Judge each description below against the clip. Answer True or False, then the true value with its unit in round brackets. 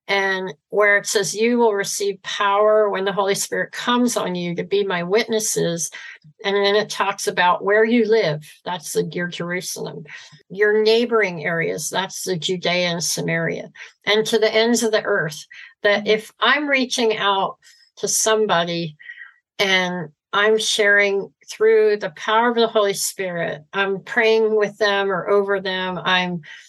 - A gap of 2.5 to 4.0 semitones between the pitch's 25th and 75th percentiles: True (3.2 semitones)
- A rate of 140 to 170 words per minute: True (160 wpm)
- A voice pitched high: True (200 Hz)